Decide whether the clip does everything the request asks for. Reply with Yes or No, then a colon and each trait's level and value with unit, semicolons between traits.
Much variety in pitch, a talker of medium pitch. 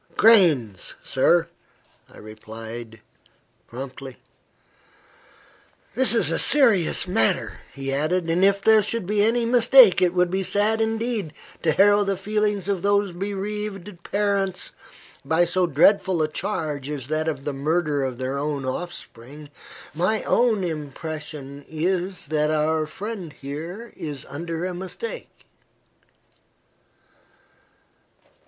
Yes: wide, 5.7 semitones; medium, 175 Hz